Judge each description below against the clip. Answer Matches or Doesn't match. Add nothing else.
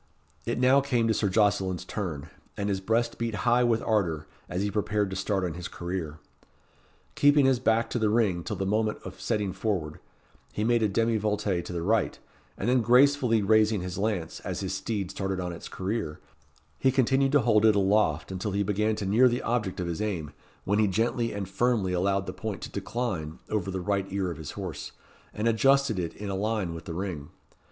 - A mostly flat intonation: Doesn't match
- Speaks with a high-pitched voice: Doesn't match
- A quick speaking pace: Matches